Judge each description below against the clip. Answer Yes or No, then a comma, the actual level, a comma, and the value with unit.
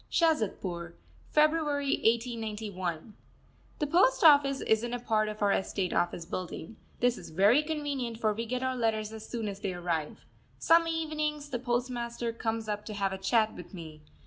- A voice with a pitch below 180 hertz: No, high, 230 Hz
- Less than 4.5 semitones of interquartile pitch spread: No, average, 5.3 semitones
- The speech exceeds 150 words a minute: Yes, average, 170 wpm